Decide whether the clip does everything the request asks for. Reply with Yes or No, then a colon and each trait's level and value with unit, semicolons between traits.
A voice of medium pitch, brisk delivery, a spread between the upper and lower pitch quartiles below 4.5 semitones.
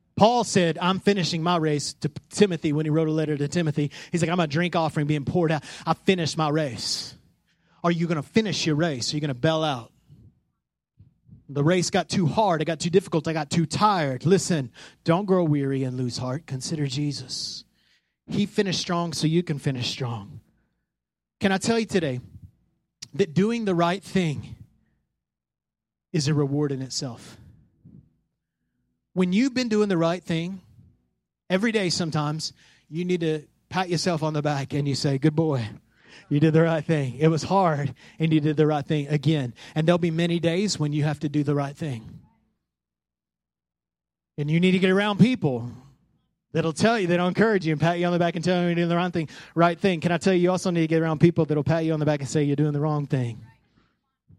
Yes: medium, 160 Hz; fast, 210 wpm; average, 3.5 semitones